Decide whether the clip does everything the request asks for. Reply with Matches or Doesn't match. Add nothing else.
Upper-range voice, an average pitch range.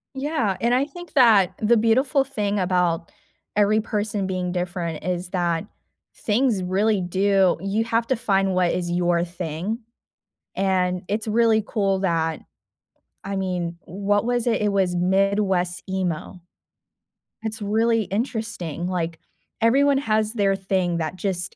Matches